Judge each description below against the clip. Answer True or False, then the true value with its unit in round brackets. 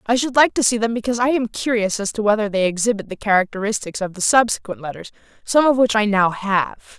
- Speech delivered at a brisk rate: True (230 wpm)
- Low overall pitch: False (215 Hz)